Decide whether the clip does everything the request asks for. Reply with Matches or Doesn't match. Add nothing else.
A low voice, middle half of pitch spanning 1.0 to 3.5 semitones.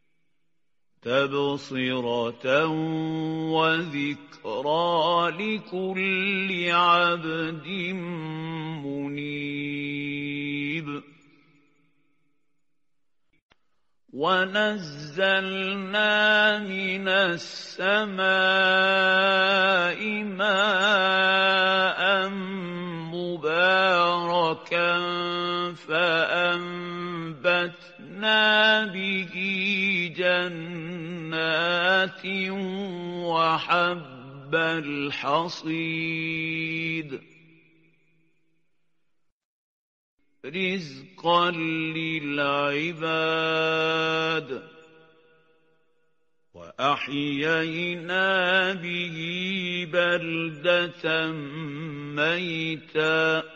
Doesn't match